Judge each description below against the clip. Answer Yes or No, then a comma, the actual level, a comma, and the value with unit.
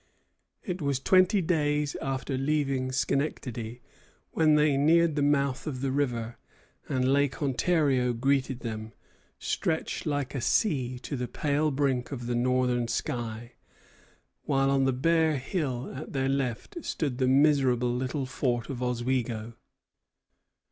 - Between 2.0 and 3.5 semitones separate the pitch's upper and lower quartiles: Yes, average, 2.8 semitones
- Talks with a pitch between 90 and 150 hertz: Yes, low, 135 Hz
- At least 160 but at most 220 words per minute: No, slow, 135 wpm